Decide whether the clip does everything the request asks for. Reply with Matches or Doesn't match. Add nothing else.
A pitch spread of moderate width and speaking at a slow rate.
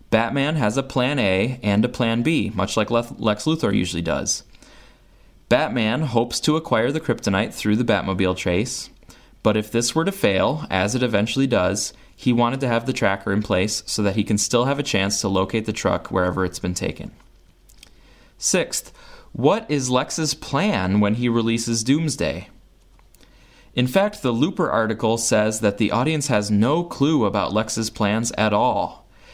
Doesn't match